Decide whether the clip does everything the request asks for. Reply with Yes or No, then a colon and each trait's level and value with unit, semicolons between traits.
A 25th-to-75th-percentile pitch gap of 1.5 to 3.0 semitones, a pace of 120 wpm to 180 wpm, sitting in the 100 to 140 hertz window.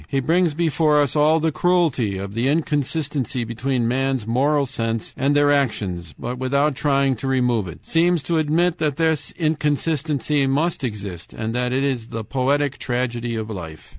No: average, 4.2 semitones; average, 170 wpm; low, 135 Hz